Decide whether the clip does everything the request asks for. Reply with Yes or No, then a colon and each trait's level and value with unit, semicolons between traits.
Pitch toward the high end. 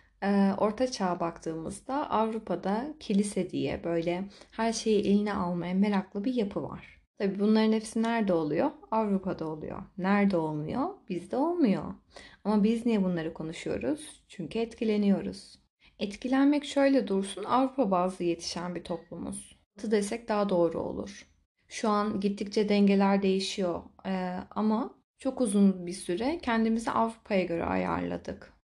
Yes: high, 200 Hz